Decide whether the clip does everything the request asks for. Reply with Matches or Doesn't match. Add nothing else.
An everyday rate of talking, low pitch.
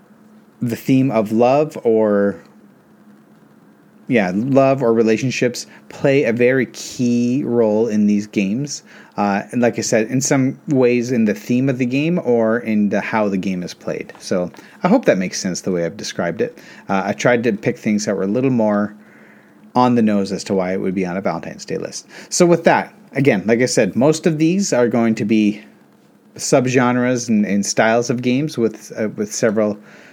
Matches